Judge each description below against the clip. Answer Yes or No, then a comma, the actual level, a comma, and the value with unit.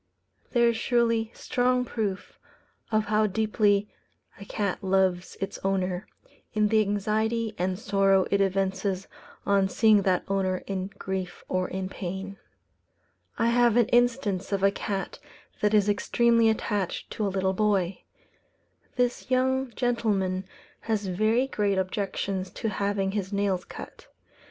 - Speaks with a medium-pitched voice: No, high, 200 Hz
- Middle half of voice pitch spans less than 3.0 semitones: Yes, narrow, 2.5 semitones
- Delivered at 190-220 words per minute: No, slow, 135 wpm